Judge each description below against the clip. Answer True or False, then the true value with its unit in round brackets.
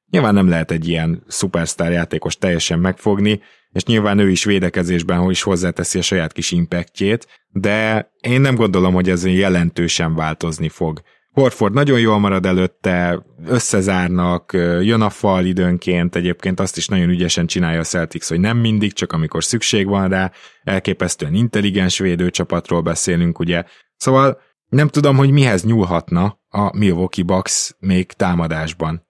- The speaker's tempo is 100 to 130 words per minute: False (150 wpm)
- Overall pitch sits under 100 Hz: True (90 Hz)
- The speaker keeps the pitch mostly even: False (3.1 semitones)